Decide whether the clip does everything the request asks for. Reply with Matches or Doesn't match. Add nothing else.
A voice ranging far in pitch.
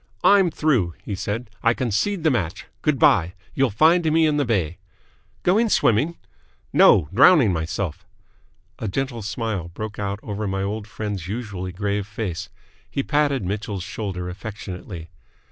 Matches